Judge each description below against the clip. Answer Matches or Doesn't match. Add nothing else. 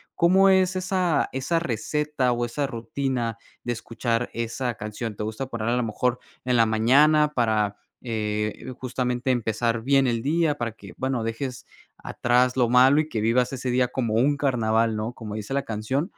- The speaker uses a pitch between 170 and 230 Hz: Doesn't match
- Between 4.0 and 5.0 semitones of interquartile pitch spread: Doesn't match